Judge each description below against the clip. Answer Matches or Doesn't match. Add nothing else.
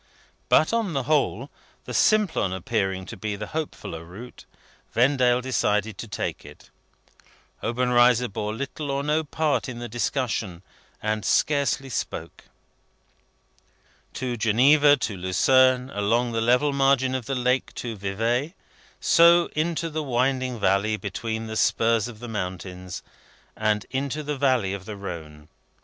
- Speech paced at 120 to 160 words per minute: Matches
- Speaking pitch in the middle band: Doesn't match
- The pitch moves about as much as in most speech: Matches